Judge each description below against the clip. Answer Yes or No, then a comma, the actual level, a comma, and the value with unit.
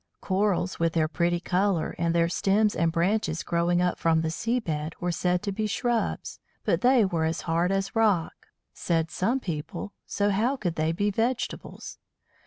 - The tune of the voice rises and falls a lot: No, average, 3.8 semitones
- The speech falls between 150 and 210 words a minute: Yes, average, 180 wpm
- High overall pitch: No, medium, 180 Hz